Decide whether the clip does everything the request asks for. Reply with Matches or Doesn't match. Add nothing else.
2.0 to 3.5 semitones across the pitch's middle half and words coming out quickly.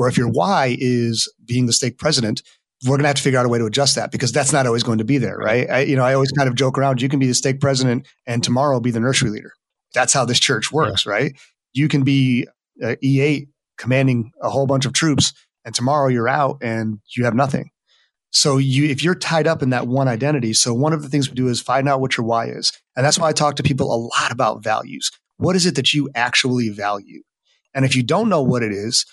Matches